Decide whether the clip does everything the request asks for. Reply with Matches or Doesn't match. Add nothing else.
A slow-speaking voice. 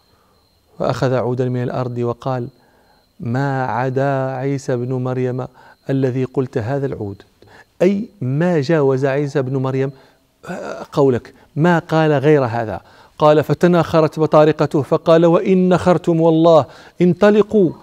Matches